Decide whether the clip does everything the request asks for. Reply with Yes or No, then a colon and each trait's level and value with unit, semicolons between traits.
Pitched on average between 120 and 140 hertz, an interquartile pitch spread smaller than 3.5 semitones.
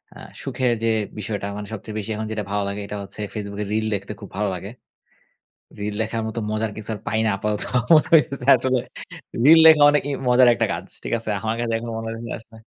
No: low, 110 Hz; narrow, 2.5 semitones